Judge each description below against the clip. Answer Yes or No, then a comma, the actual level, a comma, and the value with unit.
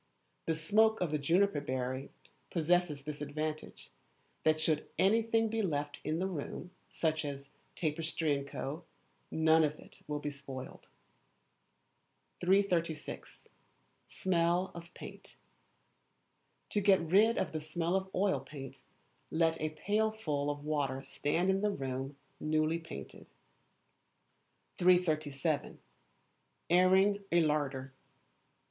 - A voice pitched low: No, medium, 160 Hz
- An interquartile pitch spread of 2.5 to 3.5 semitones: No, average, 3.9 semitones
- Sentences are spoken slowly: Yes, slow, 115 wpm